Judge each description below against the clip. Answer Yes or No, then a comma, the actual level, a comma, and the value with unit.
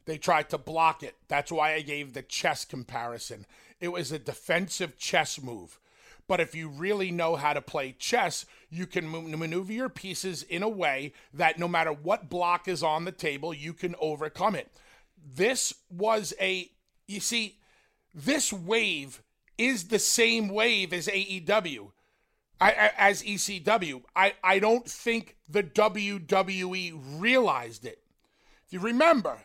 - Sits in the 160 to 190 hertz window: Yes, medium, 185 Hz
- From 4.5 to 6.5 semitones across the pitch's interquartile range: Yes, average, 4.8 semitones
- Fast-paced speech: No, average, 155 wpm